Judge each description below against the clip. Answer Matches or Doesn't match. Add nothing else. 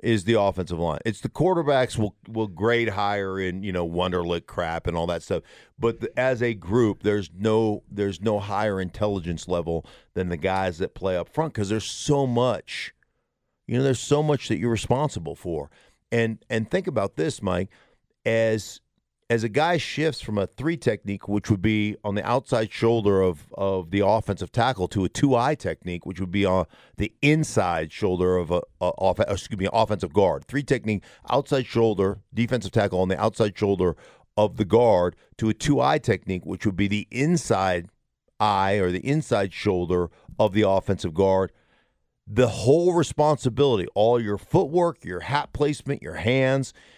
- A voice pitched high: Doesn't match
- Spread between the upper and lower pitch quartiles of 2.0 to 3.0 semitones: Doesn't match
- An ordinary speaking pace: Matches